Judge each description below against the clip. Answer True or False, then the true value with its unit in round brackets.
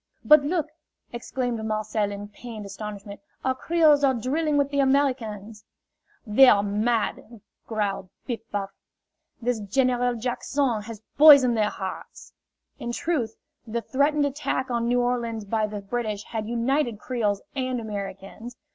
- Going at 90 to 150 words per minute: True (140 wpm)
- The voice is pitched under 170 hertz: False (235 Hz)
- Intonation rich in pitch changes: False (3.8 semitones)